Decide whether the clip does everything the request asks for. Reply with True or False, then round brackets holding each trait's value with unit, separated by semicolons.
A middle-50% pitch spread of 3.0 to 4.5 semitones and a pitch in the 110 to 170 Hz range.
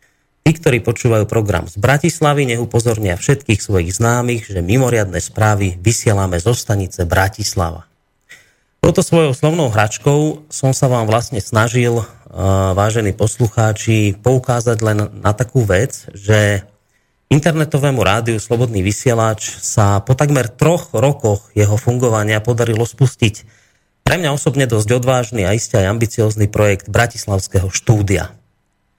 True (3.7 semitones; 115 Hz)